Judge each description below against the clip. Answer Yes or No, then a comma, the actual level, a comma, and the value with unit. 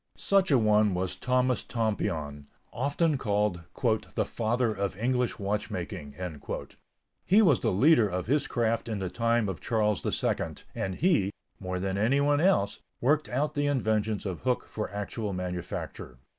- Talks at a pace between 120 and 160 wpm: Yes, average, 150 wpm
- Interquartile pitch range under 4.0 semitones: No, average, 4.9 semitones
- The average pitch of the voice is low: Yes, low, 110 Hz